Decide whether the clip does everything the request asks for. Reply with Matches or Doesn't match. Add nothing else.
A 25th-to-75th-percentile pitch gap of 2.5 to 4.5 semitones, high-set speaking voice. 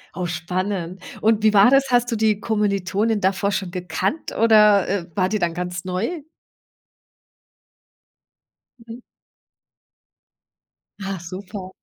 Matches